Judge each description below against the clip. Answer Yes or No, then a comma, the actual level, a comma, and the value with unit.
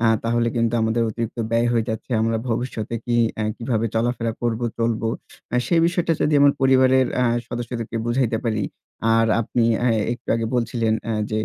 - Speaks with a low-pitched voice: Yes, low, 115 Hz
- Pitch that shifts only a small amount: Yes, narrow, 1.5 semitones